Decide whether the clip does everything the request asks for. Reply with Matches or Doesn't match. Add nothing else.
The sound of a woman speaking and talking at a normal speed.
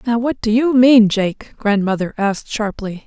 Matches